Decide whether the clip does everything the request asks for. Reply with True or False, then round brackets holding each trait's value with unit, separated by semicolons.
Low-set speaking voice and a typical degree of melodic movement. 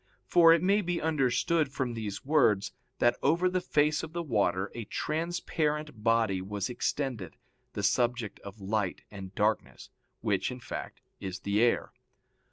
False (120 Hz; 7.1 semitones)